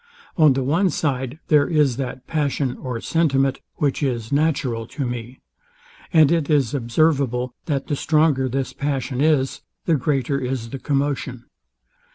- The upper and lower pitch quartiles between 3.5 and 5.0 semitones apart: No, average, 2.9 semitones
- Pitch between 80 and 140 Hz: Yes, low, 135 Hz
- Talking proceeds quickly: No, average, 150 wpm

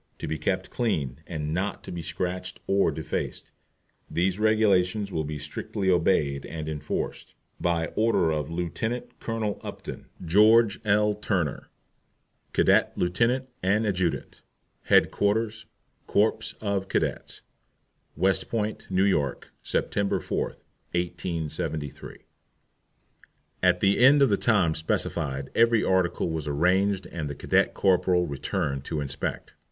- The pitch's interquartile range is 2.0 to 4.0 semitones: No, average, 4.7 semitones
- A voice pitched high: No, very low, 95 Hz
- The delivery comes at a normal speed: No, slow, 125 wpm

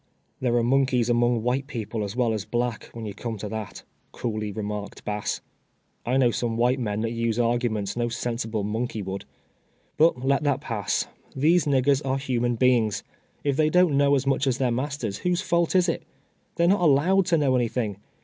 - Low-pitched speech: Yes, low, 120 Hz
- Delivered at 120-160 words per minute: No, fast, 205 wpm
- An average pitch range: Yes, average, 3.7 semitones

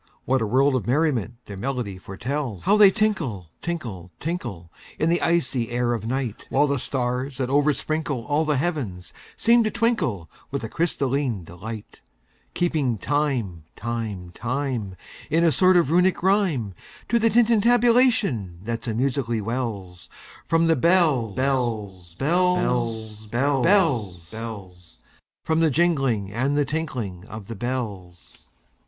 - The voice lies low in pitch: Yes, low, 130 Hz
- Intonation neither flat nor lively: No, wide, 6.9 semitones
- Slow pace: Yes, slow, 120 wpm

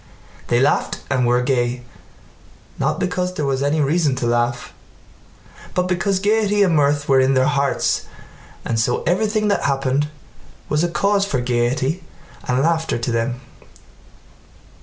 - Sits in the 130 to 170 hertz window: Yes, medium, 140 Hz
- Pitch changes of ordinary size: No, wide, 6.3 semitones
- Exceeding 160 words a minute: No, average, 145 wpm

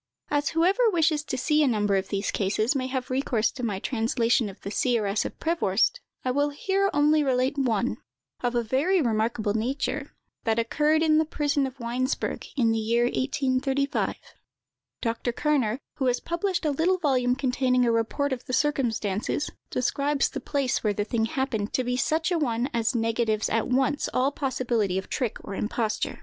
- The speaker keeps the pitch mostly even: No, average, 4.2 semitones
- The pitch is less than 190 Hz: No, very high, 255 Hz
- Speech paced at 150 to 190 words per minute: Yes, average, 180 wpm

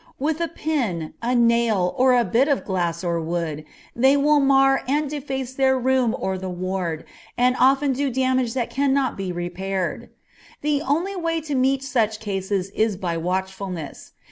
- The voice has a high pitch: Yes, high, 240 Hz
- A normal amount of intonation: No, wide, 6.3 semitones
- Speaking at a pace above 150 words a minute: Yes, average, 170 wpm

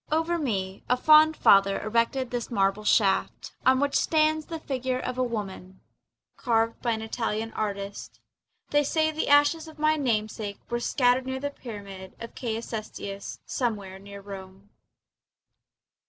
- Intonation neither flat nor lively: No, wide, 5.8 semitones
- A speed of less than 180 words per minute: Yes, average, 150 wpm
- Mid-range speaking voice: No, high, 230 Hz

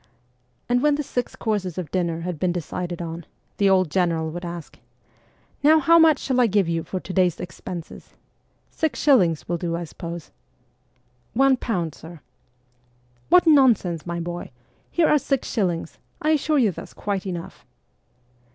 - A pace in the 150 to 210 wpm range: Yes, average, 175 wpm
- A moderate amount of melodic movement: No, wide, 6.8 semitones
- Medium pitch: Yes, medium, 180 Hz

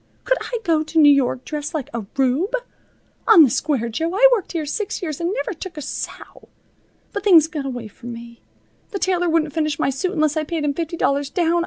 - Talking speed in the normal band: No, fast, 220 wpm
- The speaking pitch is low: No, very high, 310 Hz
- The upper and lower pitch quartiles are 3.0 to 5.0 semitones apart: Yes, average, 4.0 semitones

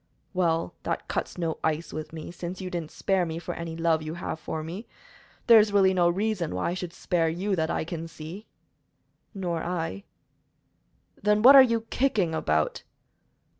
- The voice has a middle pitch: Yes, medium, 175 Hz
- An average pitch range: Yes, average, 3.1 semitones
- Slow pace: No, average, 180 wpm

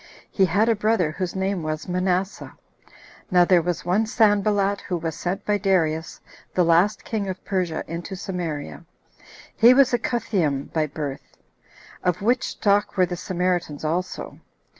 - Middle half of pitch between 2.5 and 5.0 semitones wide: Yes, average, 3.4 semitones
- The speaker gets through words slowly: No, average, 155 wpm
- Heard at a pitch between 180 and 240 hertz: Yes, medium, 185 Hz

